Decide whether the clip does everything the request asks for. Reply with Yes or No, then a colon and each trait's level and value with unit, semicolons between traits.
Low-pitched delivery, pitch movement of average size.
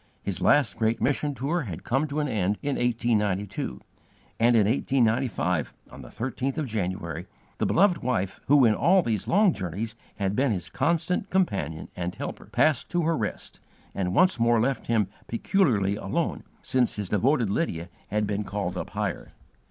No: low, 115 Hz; wide, 6.1 semitones